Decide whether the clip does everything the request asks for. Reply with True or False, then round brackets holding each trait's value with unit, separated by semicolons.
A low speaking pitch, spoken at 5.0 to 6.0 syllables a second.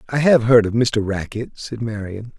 False (115 Hz; 4.7 syllables/s)